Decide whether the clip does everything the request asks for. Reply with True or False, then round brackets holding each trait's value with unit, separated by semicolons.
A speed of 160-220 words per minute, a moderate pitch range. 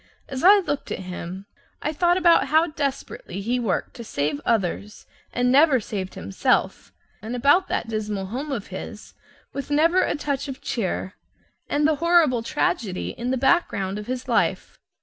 False (170 wpm; 6.5 semitones)